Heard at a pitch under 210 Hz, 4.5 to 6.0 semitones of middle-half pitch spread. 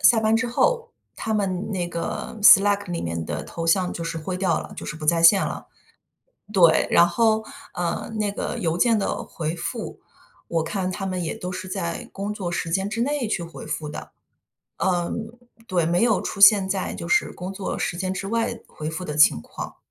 No: medium, 185 Hz; average, 3.4 semitones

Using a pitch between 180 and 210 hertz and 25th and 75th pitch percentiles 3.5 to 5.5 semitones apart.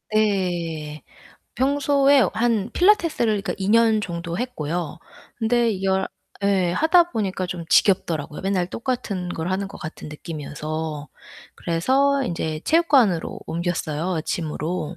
No: high, 190 Hz; wide, 6.0 semitones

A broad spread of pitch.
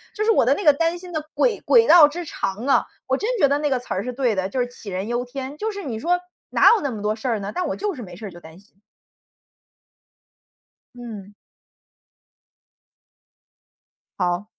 Yes: wide, 8.0 semitones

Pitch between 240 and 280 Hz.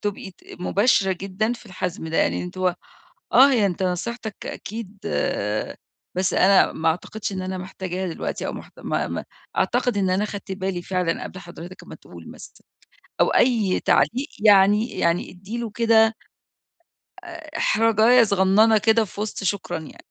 No: high, 195 Hz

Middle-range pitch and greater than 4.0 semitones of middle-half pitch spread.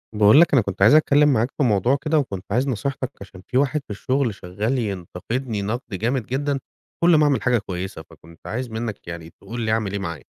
No: low, 115 Hz; wide, 5.4 semitones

